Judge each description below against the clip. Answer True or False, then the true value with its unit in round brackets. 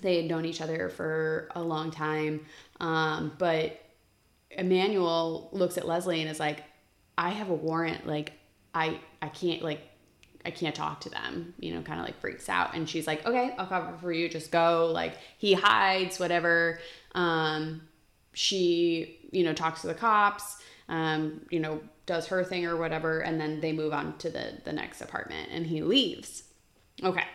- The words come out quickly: False (180 wpm)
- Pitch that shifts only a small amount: True (2.1 semitones)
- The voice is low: False (165 Hz)